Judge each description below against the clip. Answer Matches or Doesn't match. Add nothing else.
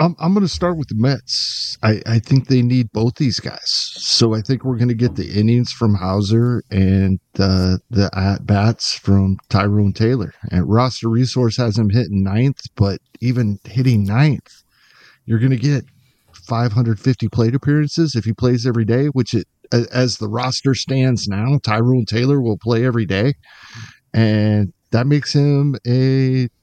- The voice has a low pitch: Matches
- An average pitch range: Matches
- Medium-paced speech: Matches